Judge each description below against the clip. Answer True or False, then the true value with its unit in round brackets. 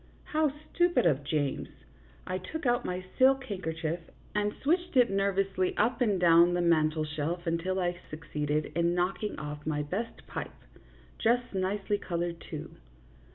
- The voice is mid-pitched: True (180 Hz)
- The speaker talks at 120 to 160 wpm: True (155 wpm)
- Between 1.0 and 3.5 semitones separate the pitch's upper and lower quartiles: False (4.4 semitones)